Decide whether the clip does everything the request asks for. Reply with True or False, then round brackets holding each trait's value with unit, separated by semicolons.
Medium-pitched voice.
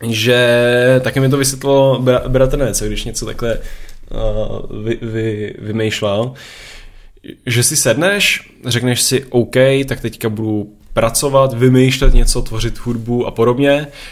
False (120 Hz)